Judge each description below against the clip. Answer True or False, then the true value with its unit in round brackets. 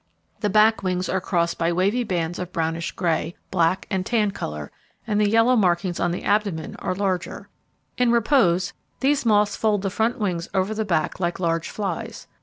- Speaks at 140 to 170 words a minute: False (185 wpm)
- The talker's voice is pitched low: False (190 Hz)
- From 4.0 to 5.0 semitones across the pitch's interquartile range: False (3.6 semitones)